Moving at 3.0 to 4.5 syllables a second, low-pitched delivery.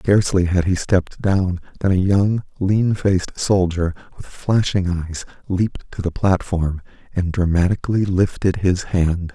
Yes: 4.4 syllables/s; very low, 95 Hz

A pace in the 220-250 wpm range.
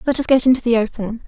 No: fast, 285 wpm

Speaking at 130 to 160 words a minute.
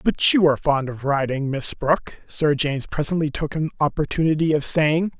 No: average, 185 wpm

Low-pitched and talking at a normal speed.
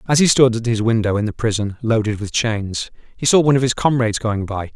No: low, 115 Hz; fast, 255 wpm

